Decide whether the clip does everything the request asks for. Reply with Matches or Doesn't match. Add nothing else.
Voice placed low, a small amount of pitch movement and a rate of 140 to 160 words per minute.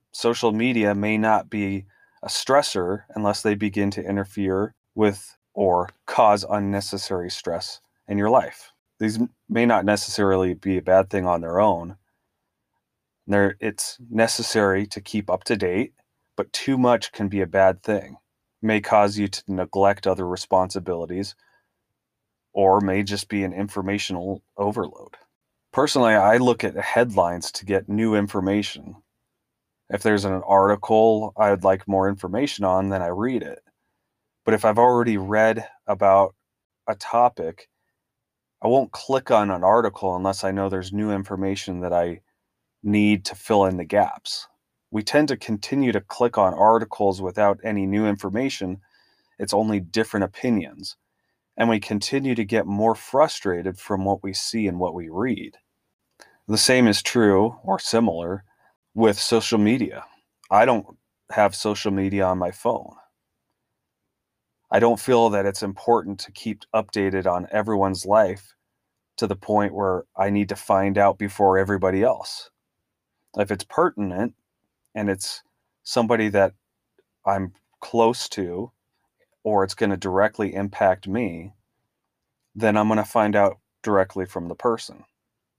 Matches